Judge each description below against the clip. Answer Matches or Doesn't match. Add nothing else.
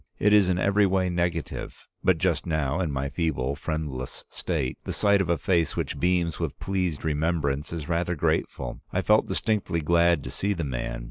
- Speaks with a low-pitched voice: Matches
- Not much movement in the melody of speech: Doesn't match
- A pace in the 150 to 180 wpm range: Doesn't match